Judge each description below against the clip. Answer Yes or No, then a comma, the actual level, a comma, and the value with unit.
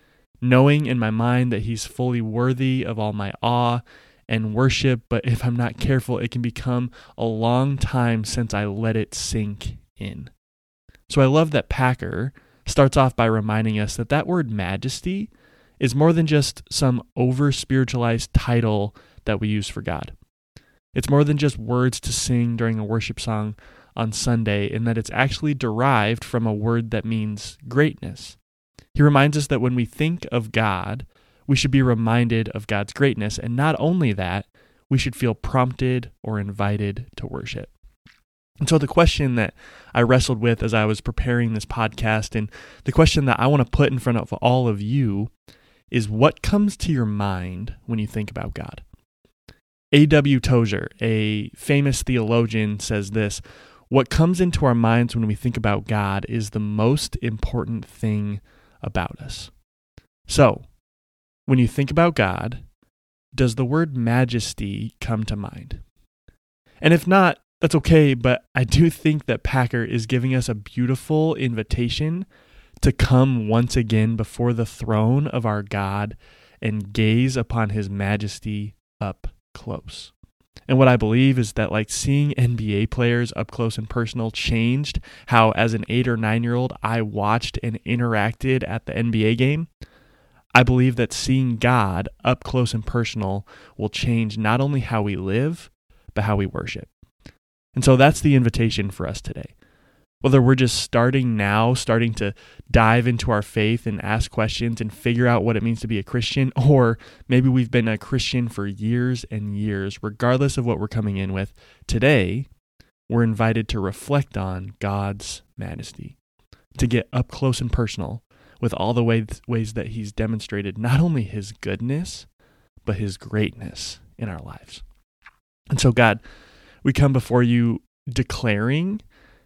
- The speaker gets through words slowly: No, average, 165 wpm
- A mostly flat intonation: No, average, 3.2 semitones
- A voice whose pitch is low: Yes, low, 115 Hz